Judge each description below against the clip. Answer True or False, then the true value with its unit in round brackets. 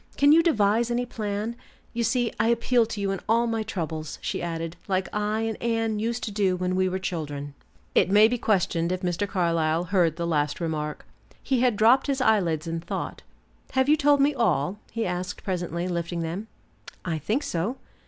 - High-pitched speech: True (200 Hz)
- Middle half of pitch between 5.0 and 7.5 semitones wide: True (5.3 semitones)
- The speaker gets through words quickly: False (195 wpm)